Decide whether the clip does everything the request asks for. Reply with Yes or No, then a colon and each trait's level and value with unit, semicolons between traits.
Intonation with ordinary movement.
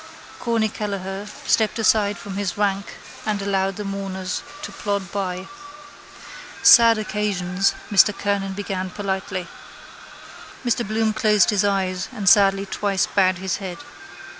No: narrow, 1.6 semitones